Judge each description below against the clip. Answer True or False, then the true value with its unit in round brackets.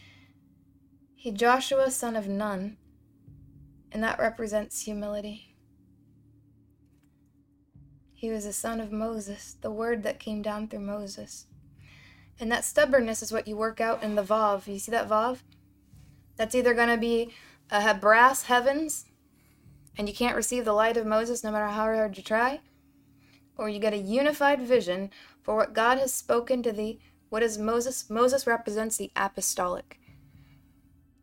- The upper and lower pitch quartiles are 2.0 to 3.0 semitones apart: False (4.6 semitones)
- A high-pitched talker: True (215 Hz)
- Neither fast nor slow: True (150 wpm)